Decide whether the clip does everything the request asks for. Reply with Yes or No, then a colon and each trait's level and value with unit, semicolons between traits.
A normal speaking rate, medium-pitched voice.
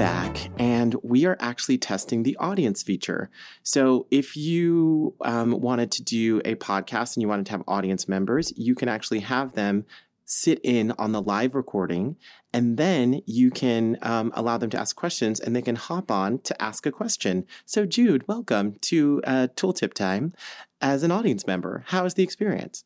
No: average, 185 wpm; low, 120 Hz